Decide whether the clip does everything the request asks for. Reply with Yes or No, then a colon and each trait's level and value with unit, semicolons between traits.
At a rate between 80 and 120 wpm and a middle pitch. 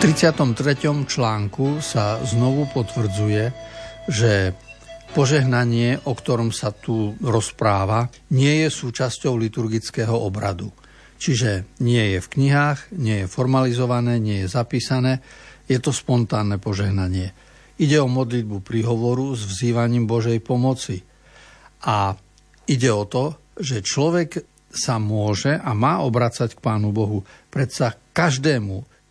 No: average, 115 wpm; low, 120 Hz